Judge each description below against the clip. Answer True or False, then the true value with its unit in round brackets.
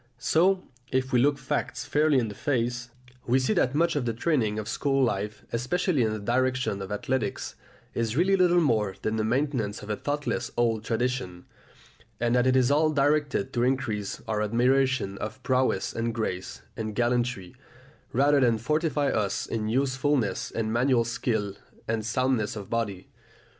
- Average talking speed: True (170 wpm)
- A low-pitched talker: True (125 Hz)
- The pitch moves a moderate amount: True (3.9 semitones)